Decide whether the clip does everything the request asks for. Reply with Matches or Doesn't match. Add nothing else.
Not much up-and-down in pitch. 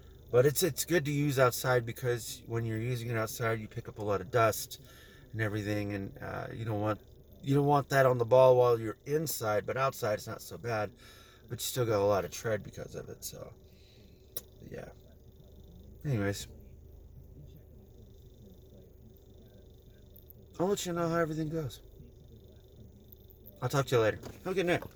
Doesn't match